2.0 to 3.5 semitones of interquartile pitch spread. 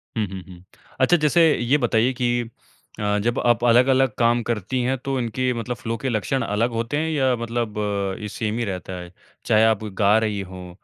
Yes: average, 3.2 semitones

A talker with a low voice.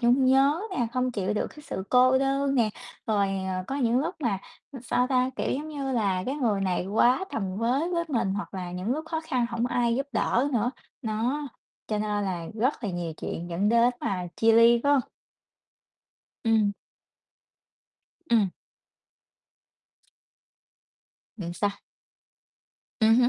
No: high, 235 Hz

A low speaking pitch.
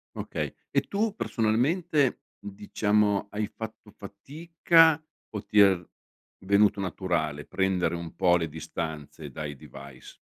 Yes: low, 100 Hz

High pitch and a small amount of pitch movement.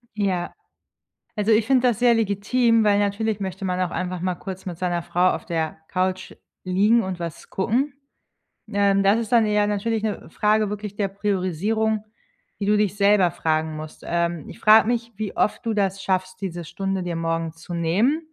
No: high, 200 Hz; average, 3.0 semitones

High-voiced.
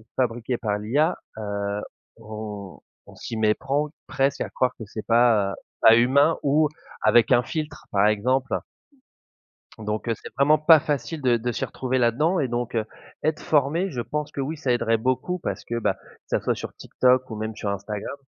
No: low, 120 Hz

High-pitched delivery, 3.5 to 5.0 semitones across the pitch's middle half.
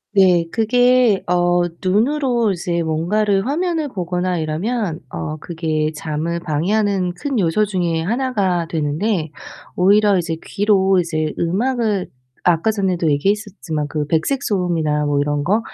No: medium, 180 Hz; average, 4.6 semitones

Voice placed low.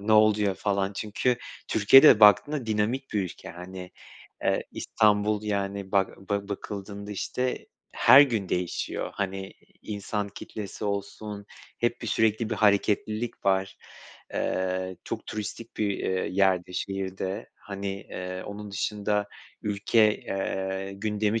Yes: low, 100 Hz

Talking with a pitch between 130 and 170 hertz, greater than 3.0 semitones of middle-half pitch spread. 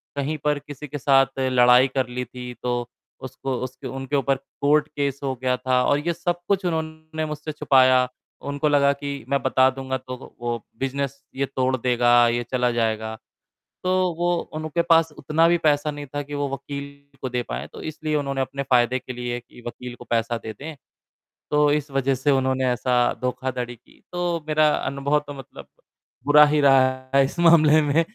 No: low, 135 Hz; average, 2.7 semitones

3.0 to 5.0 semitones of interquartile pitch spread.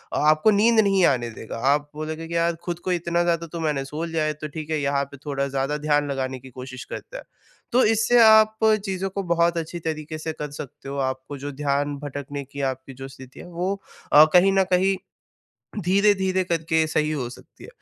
Yes: average, 4.0 semitones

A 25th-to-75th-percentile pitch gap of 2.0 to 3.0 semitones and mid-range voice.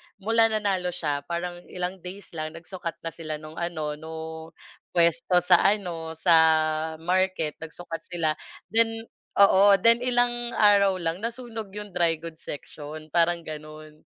No: average, 3.8 semitones; medium, 175 Hz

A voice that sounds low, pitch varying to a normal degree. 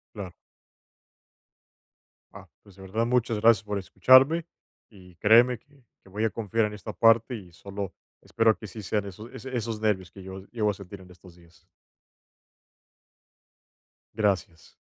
Yes: low, 105 Hz; average, 3.1 semitones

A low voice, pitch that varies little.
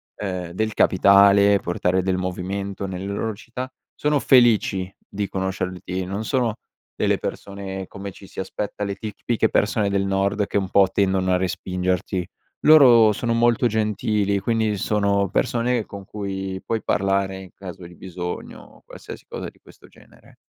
Yes: low, 100 Hz; narrow, 2.3 semitones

